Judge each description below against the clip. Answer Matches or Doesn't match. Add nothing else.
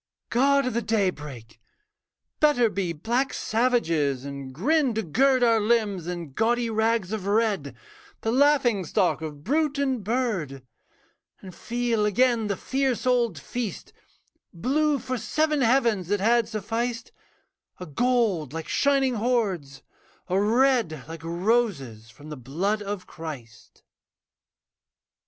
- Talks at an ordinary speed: Doesn't match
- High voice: Matches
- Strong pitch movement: Matches